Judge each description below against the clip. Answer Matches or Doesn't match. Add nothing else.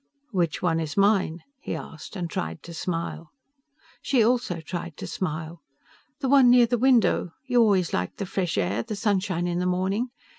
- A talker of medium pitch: Matches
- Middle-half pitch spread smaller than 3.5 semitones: Doesn't match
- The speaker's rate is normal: Matches